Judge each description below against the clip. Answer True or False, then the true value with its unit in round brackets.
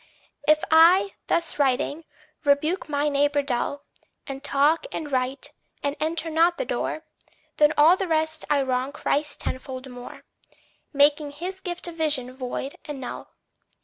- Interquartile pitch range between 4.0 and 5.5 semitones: False (2.7 semitones)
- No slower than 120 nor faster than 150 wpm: True (145 wpm)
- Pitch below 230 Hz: False (295 Hz)